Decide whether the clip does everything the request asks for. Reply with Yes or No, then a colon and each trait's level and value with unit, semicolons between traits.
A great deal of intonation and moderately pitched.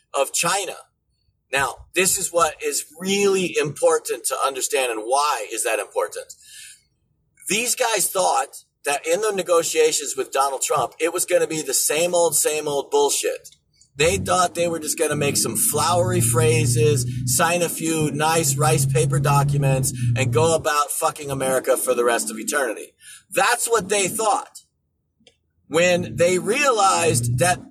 Yes: wide, 7.5 semitones; medium, 170 Hz